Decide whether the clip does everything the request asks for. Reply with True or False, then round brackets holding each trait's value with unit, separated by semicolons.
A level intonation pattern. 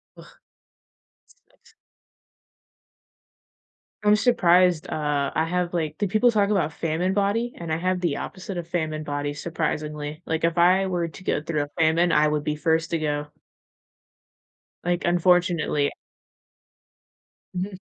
False (3.1 semitones)